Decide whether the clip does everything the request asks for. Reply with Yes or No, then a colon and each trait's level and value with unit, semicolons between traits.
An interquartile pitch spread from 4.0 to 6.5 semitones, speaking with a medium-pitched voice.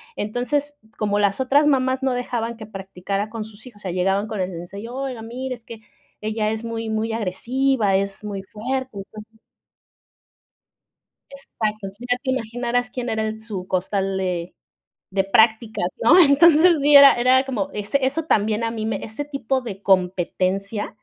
No: average, 4.4 semitones; high, 220 Hz